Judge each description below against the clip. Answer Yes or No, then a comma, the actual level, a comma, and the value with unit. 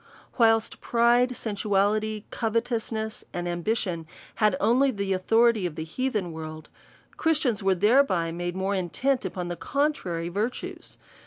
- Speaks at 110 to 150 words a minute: Yes, slow, 135 wpm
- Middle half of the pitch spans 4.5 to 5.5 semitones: Yes, average, 4.9 semitones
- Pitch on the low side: No, high, 210 Hz